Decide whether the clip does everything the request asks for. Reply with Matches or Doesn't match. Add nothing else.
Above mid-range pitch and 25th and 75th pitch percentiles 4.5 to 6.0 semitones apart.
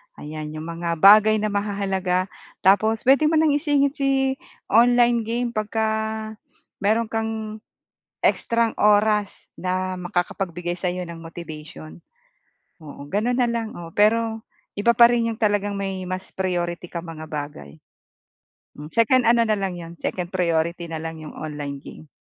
Matches